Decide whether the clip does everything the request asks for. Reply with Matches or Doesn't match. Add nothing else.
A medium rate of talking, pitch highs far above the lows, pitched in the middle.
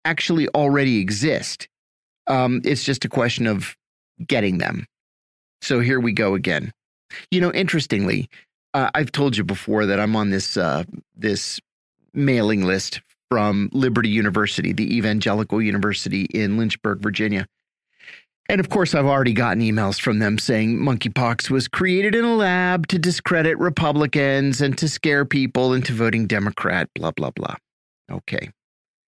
Doesn't match